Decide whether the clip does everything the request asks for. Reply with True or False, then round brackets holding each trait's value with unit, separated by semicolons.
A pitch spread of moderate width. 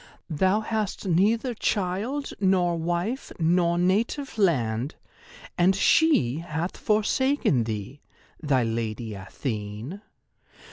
False (8.6 semitones)